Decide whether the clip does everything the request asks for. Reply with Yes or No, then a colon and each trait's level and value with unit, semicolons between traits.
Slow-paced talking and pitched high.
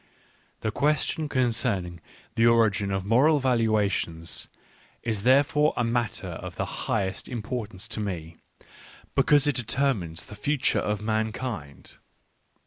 No: slow, 120 wpm; low, 115 Hz